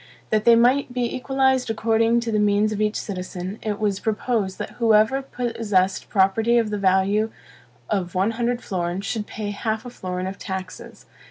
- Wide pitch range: No, average, 3.3 semitones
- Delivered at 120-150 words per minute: No, average, 175 wpm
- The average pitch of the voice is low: No, high, 215 Hz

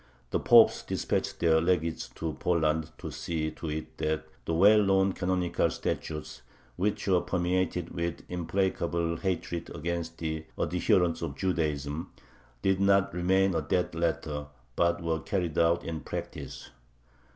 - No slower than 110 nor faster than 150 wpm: Yes, average, 140 wpm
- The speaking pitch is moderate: No, very low, 85 Hz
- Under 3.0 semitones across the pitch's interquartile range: Yes, narrow, 2.4 semitones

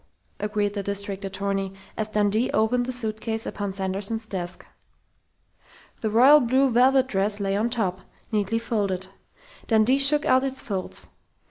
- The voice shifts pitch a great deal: No, average, 3.4 semitones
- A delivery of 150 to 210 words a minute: No, average, 140 wpm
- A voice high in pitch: Yes, high, 215 Hz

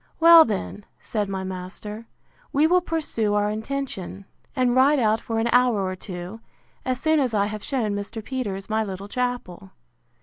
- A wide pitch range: No, average, 4.3 semitones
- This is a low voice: No, high, 220 Hz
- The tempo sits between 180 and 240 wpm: No, average, 170 wpm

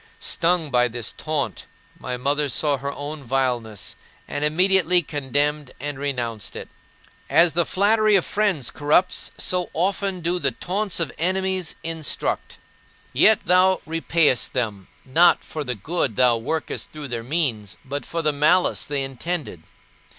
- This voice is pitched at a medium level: Yes, medium, 150 Hz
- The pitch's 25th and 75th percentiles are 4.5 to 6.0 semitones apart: Yes, average, 5.3 semitones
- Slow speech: No, average, 145 wpm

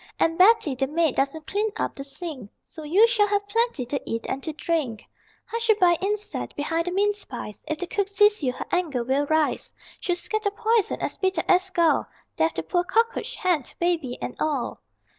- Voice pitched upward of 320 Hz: Yes, very high, 345 Hz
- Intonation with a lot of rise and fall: Yes, wide, 5.9 semitones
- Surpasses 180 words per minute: Yes, average, 195 wpm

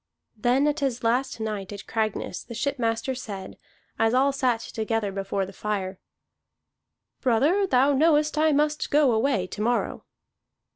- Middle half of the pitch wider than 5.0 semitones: No, average, 4.7 semitones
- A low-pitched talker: No, high, 240 Hz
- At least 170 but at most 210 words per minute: No, average, 145 wpm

